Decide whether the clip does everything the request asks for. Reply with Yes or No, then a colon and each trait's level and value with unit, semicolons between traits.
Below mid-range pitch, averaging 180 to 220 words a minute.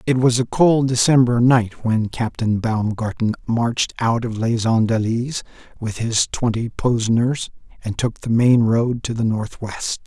No: low, 115 Hz; average, 160 wpm